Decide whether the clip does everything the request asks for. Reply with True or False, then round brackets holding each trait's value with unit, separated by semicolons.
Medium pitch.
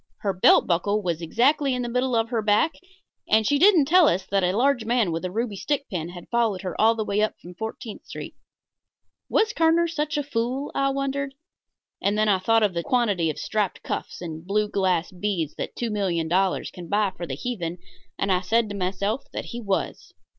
False (210 Hz)